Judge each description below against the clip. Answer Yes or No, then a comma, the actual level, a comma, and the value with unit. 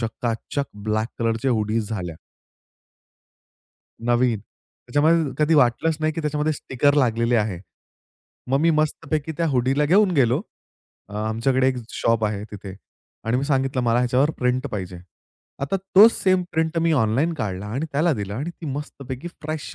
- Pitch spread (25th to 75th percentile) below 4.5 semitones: No, average, 5.3 semitones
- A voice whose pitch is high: No, low, 130 Hz